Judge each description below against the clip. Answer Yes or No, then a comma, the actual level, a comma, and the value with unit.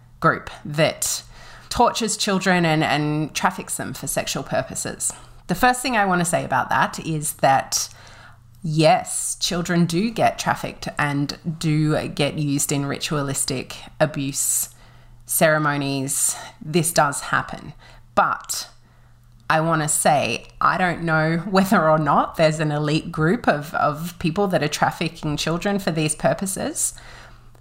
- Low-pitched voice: No, medium, 155 Hz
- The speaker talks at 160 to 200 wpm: No, slow, 135 wpm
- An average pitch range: Yes, average, 3.6 semitones